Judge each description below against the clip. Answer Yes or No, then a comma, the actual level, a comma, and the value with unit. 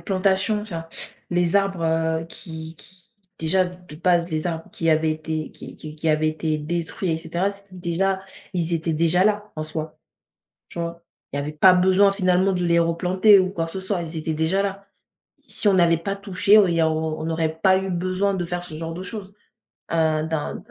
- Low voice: No, medium, 170 Hz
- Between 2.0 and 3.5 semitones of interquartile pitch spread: Yes, average, 2.8 semitones